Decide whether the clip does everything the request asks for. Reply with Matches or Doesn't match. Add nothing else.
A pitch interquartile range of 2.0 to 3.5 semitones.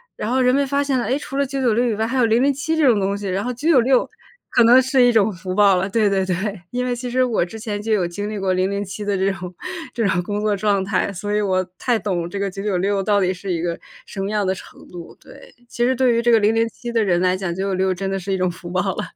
Doesn't match